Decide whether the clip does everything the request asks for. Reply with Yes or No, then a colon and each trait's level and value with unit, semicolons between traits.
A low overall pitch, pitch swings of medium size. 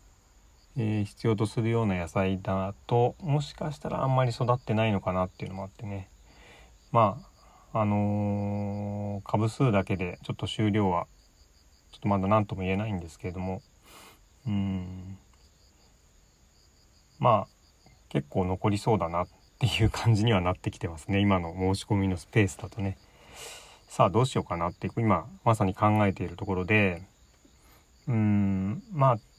Yes: low, 100 Hz; average, 3.1 semitones